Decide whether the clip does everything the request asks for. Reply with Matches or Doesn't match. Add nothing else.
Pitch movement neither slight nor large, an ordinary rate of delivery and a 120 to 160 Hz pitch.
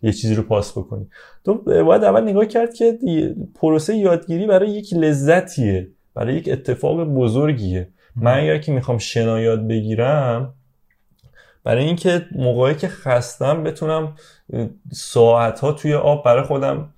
Doesn't match